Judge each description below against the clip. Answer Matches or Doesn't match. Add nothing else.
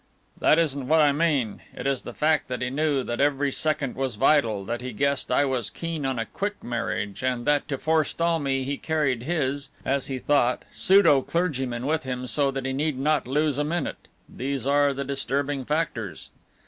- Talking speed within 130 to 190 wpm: Doesn't match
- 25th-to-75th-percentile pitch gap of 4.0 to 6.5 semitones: Doesn't match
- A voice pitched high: Doesn't match